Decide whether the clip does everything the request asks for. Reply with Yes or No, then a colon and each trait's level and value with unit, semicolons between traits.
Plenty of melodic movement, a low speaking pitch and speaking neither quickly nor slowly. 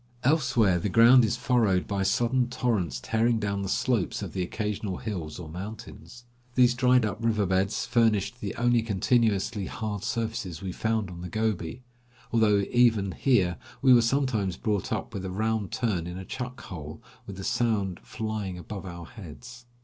No: average, 4.1 semitones; low, 110 Hz; average, 170 wpm